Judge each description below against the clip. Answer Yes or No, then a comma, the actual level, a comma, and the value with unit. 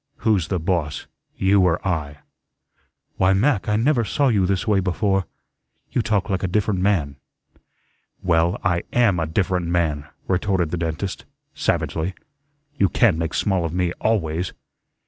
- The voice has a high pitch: No, very low, 90 Hz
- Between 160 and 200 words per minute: No, average, 150 wpm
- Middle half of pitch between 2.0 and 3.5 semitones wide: Yes, average, 3.2 semitones